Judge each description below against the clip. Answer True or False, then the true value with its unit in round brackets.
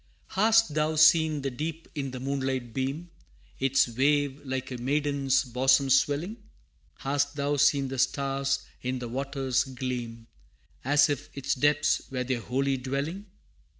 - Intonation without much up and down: True (1.9 semitones)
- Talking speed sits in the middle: True (150 wpm)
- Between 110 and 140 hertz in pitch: True (135 Hz)